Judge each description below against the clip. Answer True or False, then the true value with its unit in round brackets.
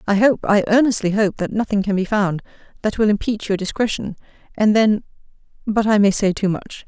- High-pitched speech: True (205 Hz)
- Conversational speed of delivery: True (190 wpm)